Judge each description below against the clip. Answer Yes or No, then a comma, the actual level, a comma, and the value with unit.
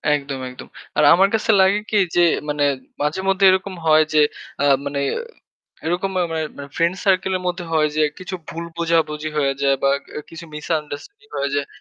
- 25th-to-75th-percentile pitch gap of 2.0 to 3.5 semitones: No, average, 4.0 semitones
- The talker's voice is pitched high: No, medium, 165 Hz